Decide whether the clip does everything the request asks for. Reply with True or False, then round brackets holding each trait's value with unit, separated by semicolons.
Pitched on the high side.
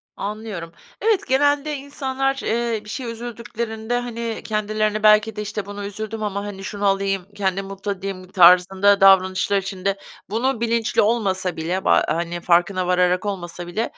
True (205 Hz)